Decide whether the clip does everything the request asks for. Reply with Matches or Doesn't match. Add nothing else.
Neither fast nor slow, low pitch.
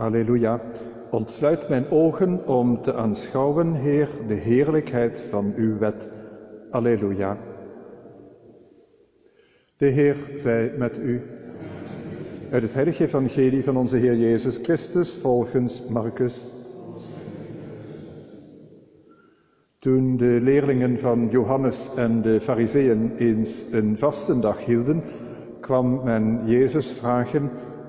Doesn't match